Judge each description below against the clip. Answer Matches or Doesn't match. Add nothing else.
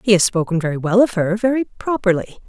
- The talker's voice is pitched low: Doesn't match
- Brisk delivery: Doesn't match